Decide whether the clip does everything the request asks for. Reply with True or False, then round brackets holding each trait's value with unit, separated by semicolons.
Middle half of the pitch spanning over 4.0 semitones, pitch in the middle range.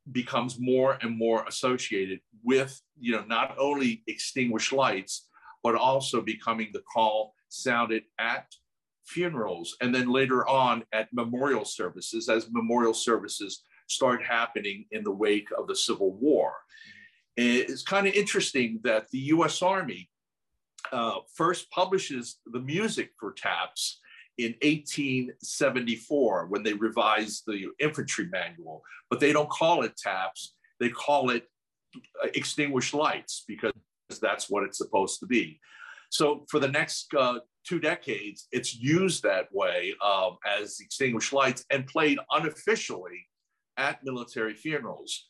False (4.4 semitones; 125 Hz)